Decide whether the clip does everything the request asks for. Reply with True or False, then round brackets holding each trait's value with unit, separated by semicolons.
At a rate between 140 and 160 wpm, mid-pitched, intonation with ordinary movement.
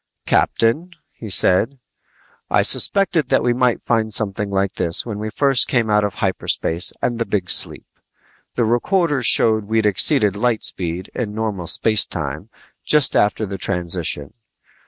False (155 wpm; 110 Hz; 3.7 semitones)